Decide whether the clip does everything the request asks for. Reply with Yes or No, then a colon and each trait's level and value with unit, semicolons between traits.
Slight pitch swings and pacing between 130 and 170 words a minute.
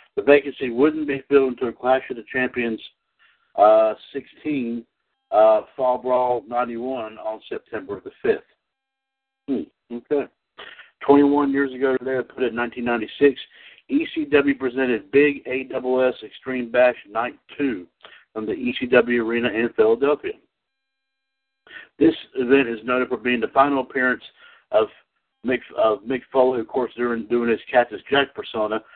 No: average, 3.2 semitones; slow, 135 wpm